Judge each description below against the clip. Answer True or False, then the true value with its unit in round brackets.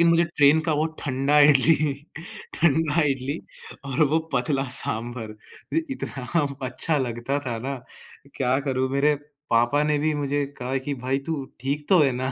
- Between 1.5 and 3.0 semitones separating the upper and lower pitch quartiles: True (2.6 semitones)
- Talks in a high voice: False (140 Hz)